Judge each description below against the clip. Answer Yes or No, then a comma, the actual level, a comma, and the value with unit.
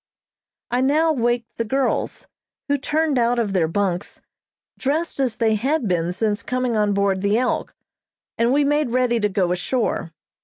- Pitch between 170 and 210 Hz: No, high, 235 Hz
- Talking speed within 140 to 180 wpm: Yes, average, 165 wpm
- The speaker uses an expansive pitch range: No, average, 4.8 semitones